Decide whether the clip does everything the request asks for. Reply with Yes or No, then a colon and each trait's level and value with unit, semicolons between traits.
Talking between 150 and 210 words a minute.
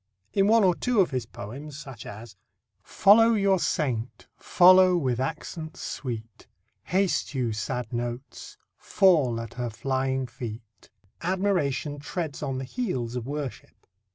No: slow, 135 wpm